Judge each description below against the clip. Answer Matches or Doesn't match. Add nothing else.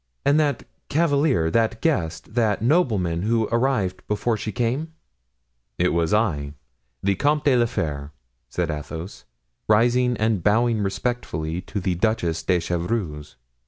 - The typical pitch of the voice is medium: Doesn't match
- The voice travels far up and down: Matches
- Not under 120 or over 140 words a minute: Matches